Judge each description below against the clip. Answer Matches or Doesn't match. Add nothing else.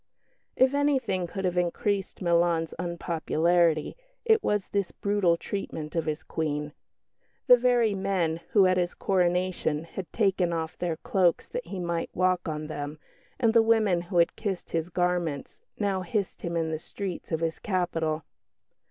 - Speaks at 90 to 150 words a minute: Doesn't match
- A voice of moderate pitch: Matches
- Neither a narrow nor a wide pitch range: Matches